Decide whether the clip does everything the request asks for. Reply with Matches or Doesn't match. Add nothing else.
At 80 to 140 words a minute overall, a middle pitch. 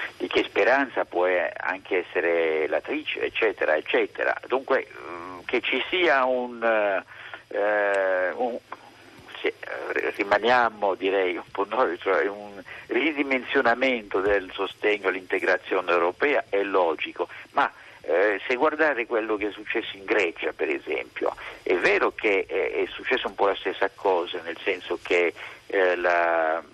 Matches